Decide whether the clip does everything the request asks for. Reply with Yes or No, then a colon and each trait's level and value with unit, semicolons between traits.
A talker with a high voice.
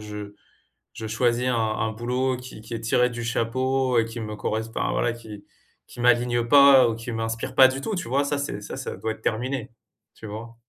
No: low, 120 Hz